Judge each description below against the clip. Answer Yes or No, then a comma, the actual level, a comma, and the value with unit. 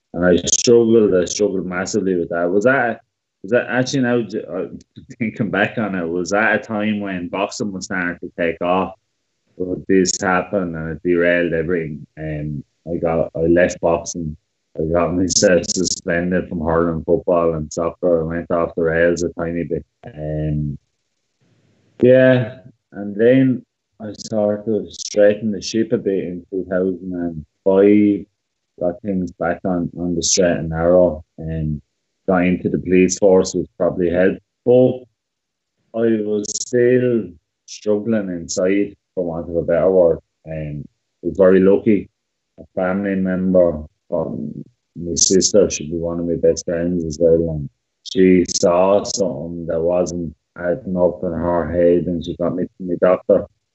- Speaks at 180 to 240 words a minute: No, average, 160 wpm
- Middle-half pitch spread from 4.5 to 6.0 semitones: No, average, 3.3 semitones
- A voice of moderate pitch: No, very low, 90 Hz